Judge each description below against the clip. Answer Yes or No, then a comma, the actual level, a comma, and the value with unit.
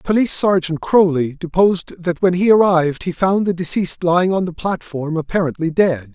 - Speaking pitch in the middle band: Yes, medium, 175 Hz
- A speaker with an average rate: Yes, average, 175 wpm